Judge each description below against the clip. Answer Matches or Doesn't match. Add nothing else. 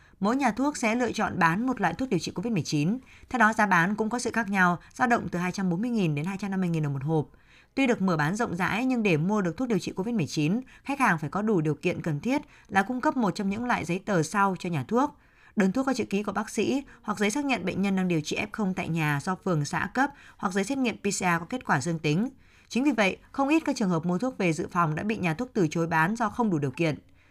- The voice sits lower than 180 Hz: Doesn't match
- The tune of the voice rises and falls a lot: Matches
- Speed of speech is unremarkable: Doesn't match